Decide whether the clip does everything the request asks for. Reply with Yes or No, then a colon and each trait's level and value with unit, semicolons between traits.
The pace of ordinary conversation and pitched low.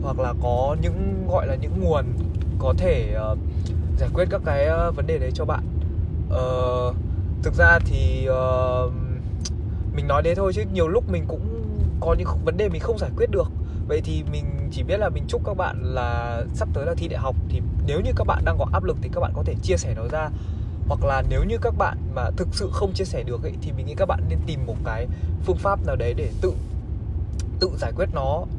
Yes: average, 235 wpm; very low, 90 Hz